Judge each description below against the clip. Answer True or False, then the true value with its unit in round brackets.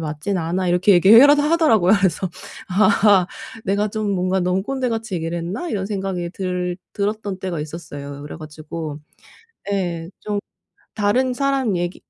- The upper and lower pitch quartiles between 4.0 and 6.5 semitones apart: False (3.6 semitones)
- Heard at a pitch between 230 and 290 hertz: False (190 Hz)